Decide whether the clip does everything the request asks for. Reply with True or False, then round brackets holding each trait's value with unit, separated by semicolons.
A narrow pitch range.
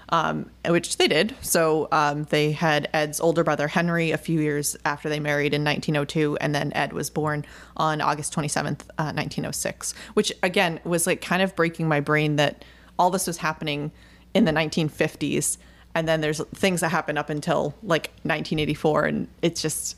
True (2.1 semitones)